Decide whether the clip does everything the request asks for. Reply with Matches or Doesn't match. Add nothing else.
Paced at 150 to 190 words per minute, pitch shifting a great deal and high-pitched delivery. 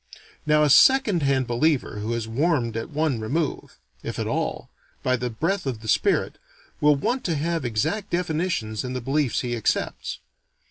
Doesn't match